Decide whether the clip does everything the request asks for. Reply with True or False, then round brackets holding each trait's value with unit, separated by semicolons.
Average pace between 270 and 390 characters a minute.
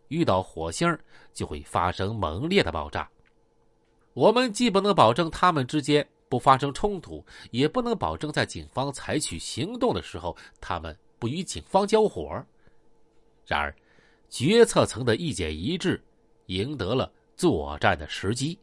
False (230 characters per minute)